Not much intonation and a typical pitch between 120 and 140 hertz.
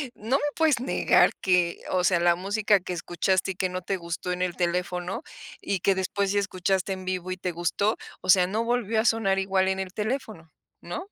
No: narrow, 2.2 semitones; high, 190 Hz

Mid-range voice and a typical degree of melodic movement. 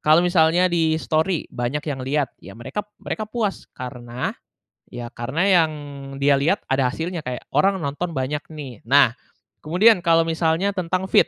Yes: medium, 155 Hz; average, 4.9 semitones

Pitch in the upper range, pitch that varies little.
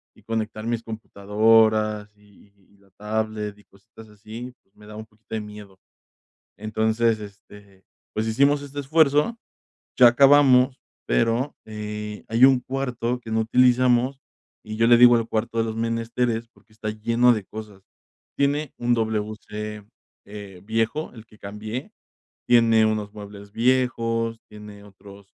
No: low, 110 Hz; narrow, 2.3 semitones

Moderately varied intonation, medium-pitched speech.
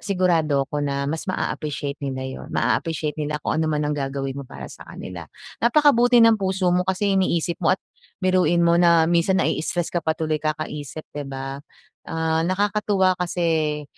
Yes: average, 3.9 semitones; medium, 160 Hz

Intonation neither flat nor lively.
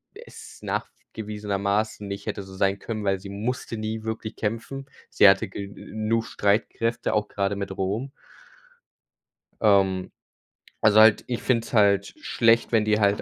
No: narrow, 2.0 semitones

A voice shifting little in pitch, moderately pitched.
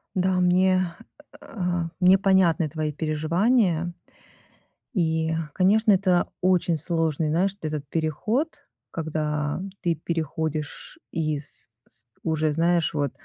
No: average, 3.0 semitones; medium, 165 Hz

